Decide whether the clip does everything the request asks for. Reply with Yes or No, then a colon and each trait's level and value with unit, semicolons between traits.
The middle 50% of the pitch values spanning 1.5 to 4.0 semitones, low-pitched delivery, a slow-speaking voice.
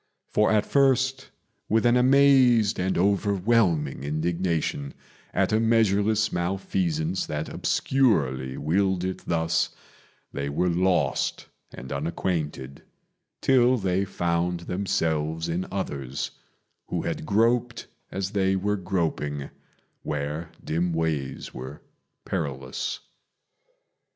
No: average, 4.9 semitones; very low, 90 Hz; slow, 100 wpm